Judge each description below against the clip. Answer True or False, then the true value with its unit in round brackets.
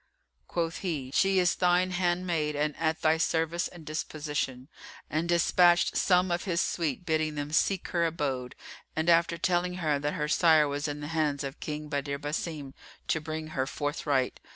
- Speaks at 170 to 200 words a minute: True (175 wpm)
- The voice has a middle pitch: True (160 Hz)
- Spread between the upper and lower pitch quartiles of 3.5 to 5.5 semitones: False (2.8 semitones)